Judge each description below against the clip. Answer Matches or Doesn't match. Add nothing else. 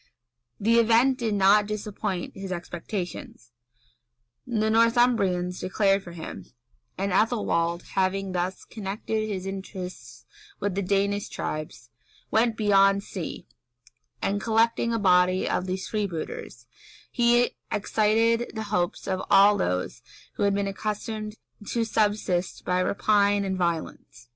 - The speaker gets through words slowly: Matches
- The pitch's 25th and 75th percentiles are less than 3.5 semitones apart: Matches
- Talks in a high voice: Matches